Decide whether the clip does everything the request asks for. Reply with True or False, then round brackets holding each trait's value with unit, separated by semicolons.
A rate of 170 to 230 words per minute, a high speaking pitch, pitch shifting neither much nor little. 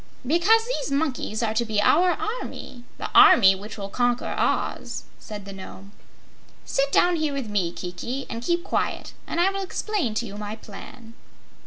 False (175 wpm; 240 Hz; 7.9 semitones)